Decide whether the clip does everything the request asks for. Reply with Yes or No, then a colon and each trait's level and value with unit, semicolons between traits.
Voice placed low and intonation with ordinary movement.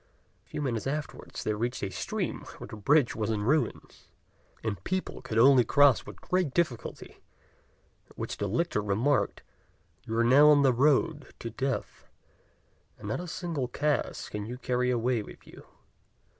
Yes: low, 125 Hz; average, 4.7 semitones